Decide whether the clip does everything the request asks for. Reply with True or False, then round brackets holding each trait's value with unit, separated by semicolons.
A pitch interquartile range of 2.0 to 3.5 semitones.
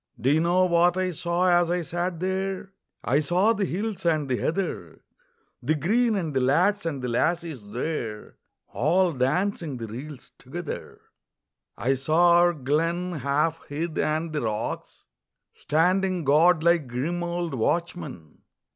False (4.2 semitones)